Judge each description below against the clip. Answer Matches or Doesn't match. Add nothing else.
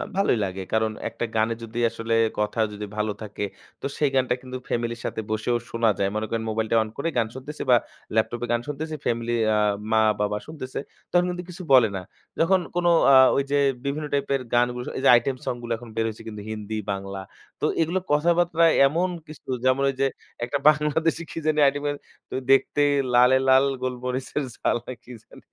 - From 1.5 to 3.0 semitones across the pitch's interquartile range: Doesn't match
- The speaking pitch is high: Doesn't match